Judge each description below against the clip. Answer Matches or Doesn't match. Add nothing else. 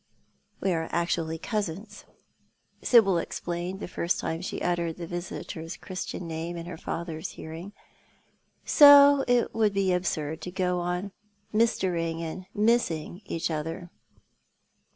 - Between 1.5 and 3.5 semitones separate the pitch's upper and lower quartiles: Matches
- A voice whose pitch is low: Doesn't match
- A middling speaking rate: Doesn't match